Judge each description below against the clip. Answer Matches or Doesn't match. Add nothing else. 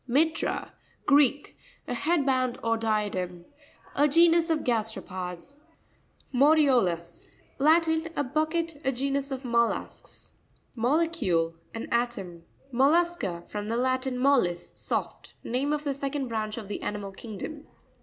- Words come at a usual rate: Doesn't match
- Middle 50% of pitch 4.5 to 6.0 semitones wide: Matches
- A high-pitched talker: Matches